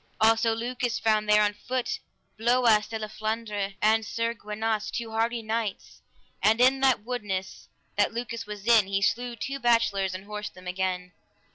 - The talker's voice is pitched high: Yes, high, 220 Hz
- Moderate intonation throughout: No, narrow, 2.0 semitones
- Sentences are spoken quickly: No, average, 165 wpm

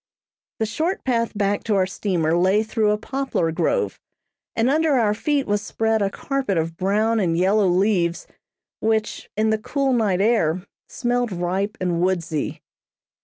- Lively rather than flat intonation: No, average, 3.8 semitones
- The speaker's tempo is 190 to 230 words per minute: No, average, 160 wpm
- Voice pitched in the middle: No, high, 210 Hz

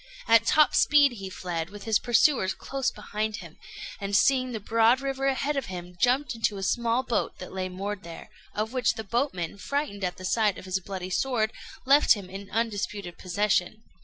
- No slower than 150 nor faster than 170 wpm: No, average, 190 wpm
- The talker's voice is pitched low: No, high, 215 Hz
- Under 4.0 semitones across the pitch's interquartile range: No, average, 4.8 semitones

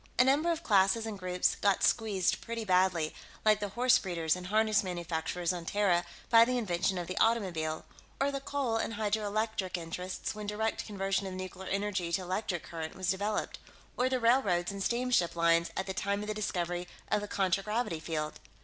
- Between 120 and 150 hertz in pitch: No, high, 195 Hz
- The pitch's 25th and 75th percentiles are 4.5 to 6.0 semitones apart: No, average, 3.6 semitones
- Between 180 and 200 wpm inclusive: Yes, average, 185 wpm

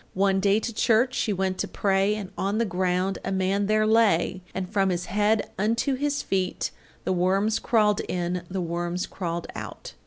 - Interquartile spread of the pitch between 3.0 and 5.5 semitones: No, narrow, 2.6 semitones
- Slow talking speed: No, average, 185 wpm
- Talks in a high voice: Yes, high, 195 Hz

